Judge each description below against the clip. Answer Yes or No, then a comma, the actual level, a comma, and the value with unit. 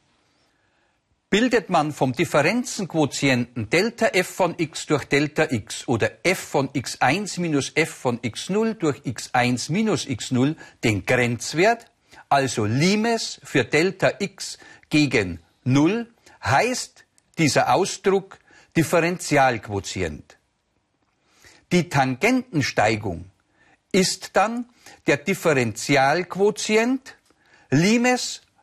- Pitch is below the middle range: No, medium, 150 Hz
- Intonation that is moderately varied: No, wide, 7.0 semitones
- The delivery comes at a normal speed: No, slow, 90 wpm